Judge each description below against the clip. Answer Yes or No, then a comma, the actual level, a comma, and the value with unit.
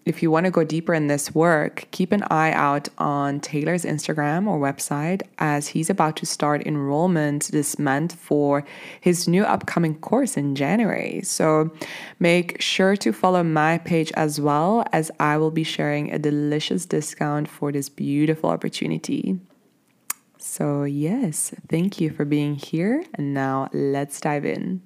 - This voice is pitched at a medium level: Yes, medium, 155 Hz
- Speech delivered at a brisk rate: No, average, 160 wpm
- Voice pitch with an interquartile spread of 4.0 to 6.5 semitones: No, average, 3.5 semitones